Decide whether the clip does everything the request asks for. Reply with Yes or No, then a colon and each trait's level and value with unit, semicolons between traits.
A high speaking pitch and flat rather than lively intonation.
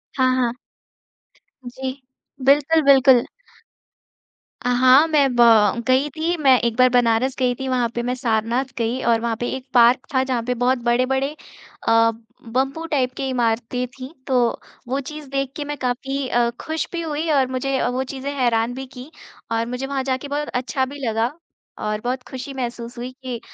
Yes: very high, 255 Hz; narrow, 2.0 semitones